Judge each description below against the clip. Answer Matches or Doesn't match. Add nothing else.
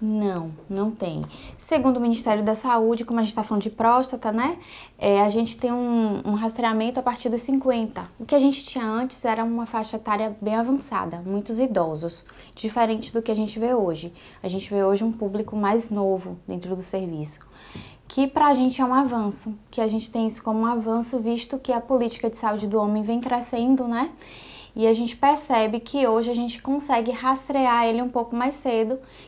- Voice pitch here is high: Matches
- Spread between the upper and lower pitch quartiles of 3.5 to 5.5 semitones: Doesn't match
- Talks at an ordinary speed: Doesn't match